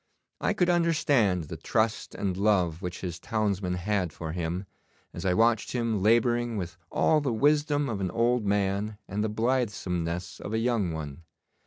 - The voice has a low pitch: Yes, low, 105 Hz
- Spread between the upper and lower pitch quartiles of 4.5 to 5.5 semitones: Yes, average, 4.8 semitones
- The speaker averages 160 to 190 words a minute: Yes, average, 170 wpm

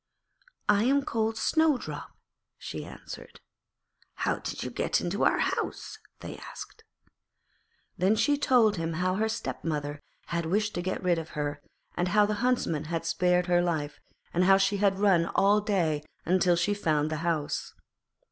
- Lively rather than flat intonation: No, average, 4.1 semitones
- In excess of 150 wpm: Yes, average, 160 wpm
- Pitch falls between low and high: Yes, medium, 180 Hz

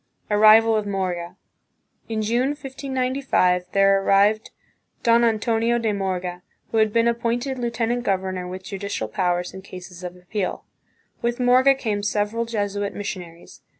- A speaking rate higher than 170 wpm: No, slow, 135 wpm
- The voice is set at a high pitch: Yes, high, 210 Hz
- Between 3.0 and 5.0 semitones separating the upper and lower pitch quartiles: Yes, average, 3.9 semitones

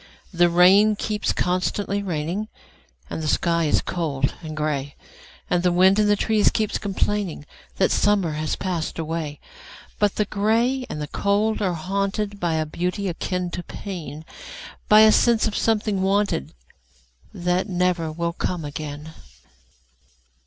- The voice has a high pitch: No, medium, 180 Hz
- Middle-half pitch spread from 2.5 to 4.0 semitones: No, average, 4.7 semitones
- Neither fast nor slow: No, slow, 130 wpm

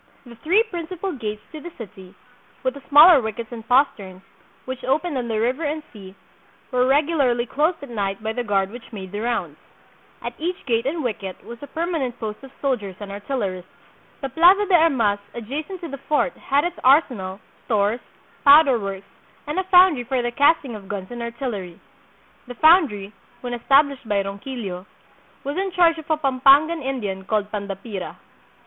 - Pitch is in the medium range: No, very high, 250 Hz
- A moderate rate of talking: Yes, average, 180 wpm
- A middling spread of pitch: No, wide, 6.4 semitones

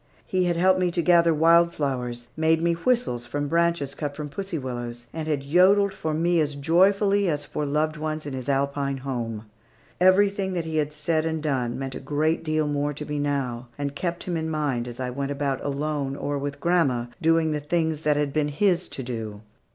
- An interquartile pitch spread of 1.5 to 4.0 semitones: Yes, average, 3.3 semitones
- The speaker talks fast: Yes, fast, 215 wpm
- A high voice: No, medium, 150 Hz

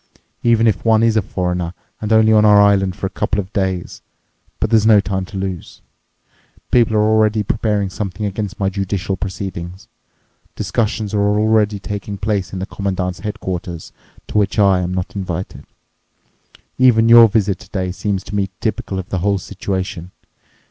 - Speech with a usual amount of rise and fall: No, narrow, 2.3 semitones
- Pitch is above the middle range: No, low, 100 Hz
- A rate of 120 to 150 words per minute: No, average, 170 wpm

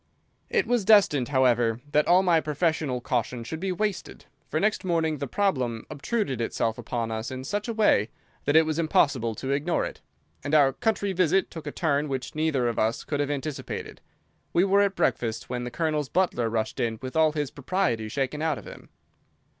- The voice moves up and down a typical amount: No, wide, 5.9 semitones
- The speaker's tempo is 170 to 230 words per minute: Yes, average, 195 wpm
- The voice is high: No, medium, 145 Hz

